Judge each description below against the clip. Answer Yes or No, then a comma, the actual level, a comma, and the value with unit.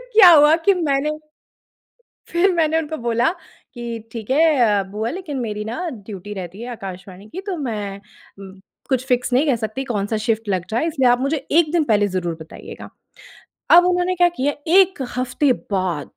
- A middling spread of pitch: No, wide, 7.1 semitones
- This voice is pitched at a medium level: No, very high, 250 Hz